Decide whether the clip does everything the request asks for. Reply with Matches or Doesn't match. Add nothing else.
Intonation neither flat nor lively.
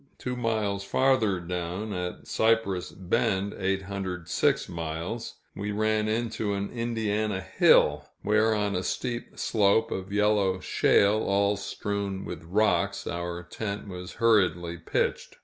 Matches